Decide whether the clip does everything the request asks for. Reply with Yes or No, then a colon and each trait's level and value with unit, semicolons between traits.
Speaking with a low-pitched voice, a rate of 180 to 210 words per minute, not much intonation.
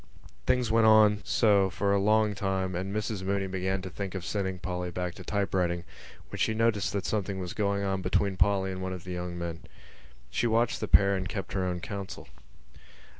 Yes: very low, 95 Hz; fast, 205 wpm; narrow, 1.9 semitones